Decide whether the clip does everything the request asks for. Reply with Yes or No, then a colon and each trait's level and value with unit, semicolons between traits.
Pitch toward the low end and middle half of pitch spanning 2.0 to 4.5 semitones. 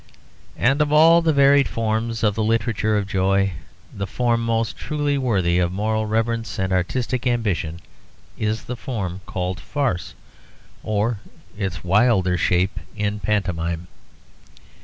Yes: low, 110 Hz; average, 3.9 semitones